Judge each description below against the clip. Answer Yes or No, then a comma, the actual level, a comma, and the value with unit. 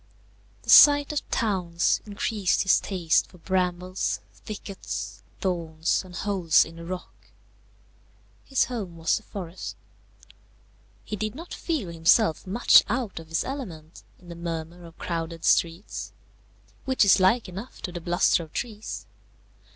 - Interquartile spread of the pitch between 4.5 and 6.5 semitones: No, average, 4.1 semitones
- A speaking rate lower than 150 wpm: Yes, average, 140 wpm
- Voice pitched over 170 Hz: Yes, medium, 185 Hz